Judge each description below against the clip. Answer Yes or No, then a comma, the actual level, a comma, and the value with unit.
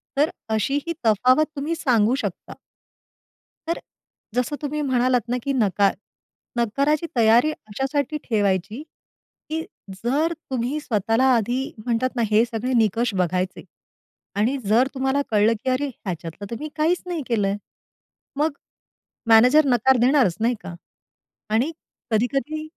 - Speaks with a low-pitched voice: No, very high, 250 Hz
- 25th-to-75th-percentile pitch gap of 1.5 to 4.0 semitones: No, average, 4.5 semitones